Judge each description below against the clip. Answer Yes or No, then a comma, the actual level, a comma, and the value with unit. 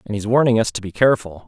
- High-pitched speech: No, low, 110 Hz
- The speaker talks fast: Yes, fast, 285 wpm